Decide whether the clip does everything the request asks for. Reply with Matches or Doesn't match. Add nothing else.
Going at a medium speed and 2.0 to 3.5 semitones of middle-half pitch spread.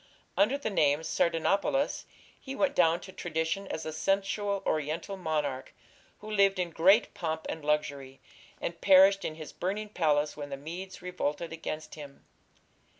Doesn't match